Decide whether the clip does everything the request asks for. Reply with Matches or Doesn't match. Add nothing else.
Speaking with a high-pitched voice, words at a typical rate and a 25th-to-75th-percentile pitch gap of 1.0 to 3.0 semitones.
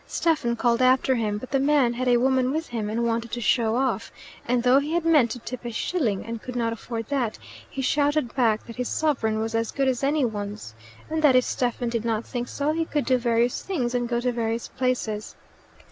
Doesn't match